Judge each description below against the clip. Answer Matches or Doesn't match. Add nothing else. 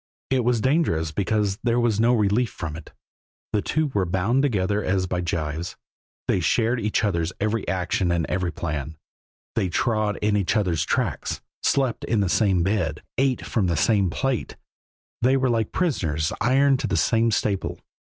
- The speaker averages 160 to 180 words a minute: Matches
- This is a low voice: Matches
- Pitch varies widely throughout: Doesn't match